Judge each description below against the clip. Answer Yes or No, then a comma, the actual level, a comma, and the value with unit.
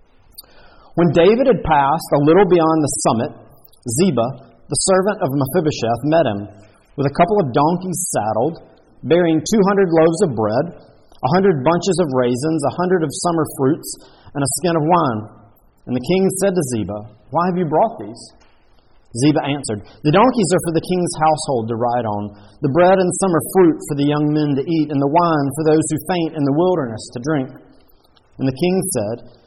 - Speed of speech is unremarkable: Yes, average, 190 wpm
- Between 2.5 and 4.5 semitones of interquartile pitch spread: No, wide, 5.4 semitones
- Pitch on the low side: No, medium, 155 Hz